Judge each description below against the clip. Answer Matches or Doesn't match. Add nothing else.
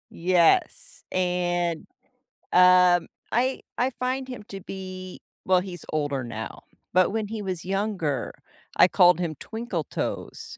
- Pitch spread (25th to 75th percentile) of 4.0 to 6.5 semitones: Doesn't match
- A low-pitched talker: Doesn't match